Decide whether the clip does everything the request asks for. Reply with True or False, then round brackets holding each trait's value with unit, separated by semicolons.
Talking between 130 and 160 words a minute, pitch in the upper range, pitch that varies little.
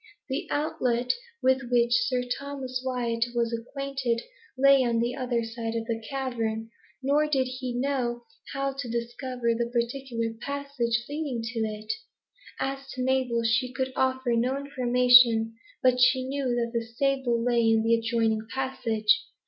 True (150 wpm; 245 Hz; 2.2 semitones)